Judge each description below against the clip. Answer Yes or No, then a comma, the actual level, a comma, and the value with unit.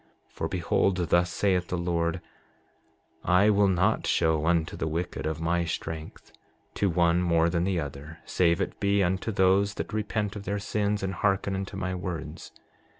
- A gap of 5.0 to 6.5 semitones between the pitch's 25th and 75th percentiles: No, average, 2.8 semitones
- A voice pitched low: Yes, very low, 90 Hz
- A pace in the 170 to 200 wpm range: Yes, average, 175 wpm